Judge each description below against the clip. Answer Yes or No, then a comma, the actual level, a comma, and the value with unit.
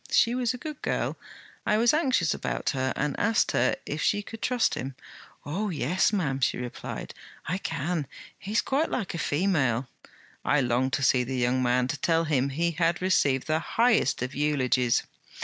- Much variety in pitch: Yes, wide, 7.5 semitones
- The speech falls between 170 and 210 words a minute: Yes, average, 185 wpm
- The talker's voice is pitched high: No, medium, 155 Hz